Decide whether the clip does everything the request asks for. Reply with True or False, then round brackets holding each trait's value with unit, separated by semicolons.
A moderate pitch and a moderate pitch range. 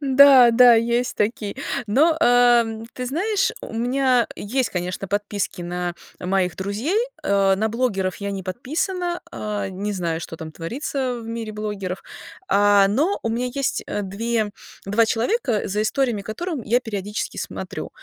False (225 Hz; 4.1 semitones)